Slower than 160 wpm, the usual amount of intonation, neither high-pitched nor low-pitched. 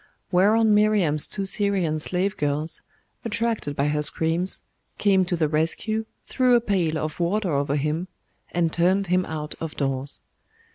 Yes: average, 150 wpm; average, 4.8 semitones; medium, 175 Hz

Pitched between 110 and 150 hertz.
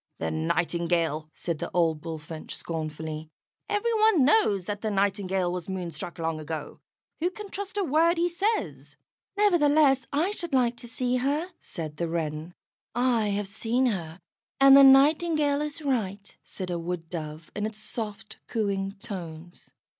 No: high, 205 Hz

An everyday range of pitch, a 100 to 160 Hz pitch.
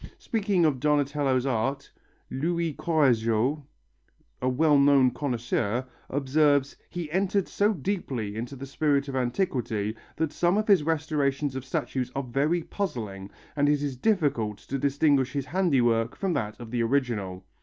Yes: average, 4.2 semitones; medium, 140 Hz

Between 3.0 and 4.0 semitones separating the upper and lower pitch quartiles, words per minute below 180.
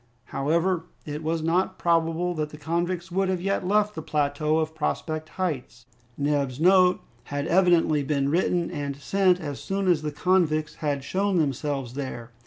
Yes: average, 3.7 semitones; average, 165 wpm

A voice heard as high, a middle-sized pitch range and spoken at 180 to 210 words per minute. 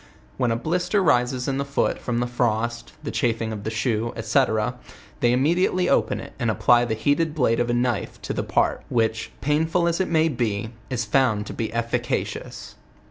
No: low, 120 Hz; average, 4.0 semitones; average, 195 wpm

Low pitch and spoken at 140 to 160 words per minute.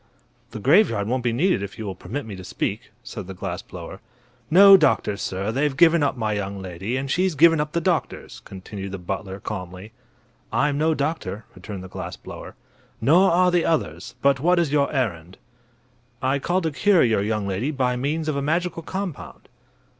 No: low, 130 Hz; average, 190 wpm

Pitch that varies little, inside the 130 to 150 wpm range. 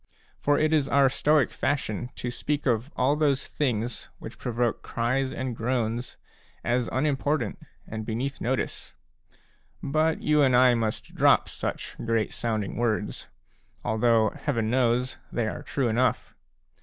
No: average, 3.2 semitones; average, 140 wpm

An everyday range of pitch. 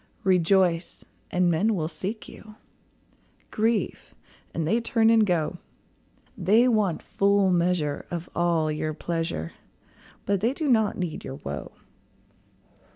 Yes: average, 4.6 semitones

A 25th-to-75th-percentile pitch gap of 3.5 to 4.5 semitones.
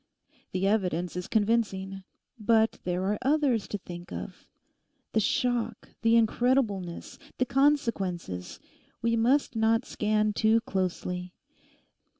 Yes: average, 3.8 semitones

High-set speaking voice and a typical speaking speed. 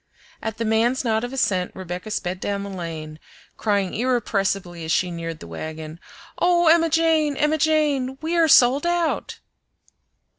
Yes: high, 220 Hz; average, 155 wpm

